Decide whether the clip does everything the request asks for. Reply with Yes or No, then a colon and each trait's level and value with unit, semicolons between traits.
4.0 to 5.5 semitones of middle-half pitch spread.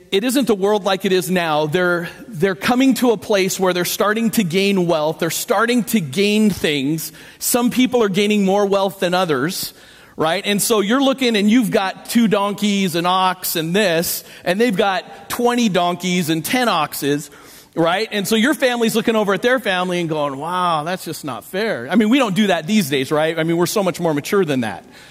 Yes: average, 4.4 semitones